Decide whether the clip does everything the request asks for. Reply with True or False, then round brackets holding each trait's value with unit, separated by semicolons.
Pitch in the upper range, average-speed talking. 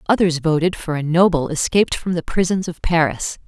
False (165 Hz; 190 wpm)